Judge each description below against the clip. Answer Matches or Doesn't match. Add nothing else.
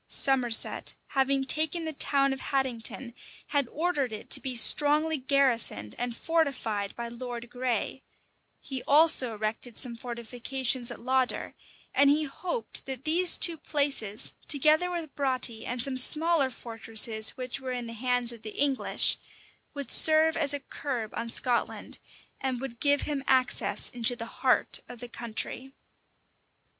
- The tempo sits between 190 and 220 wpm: Doesn't match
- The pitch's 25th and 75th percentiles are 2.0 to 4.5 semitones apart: Matches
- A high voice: Matches